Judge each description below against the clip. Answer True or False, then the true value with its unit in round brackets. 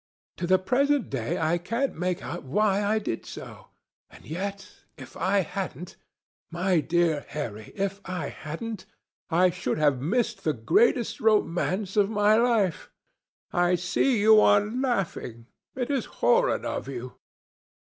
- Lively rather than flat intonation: False (4.7 semitones)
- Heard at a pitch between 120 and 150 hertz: False (190 Hz)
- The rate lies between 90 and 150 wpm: True (140 wpm)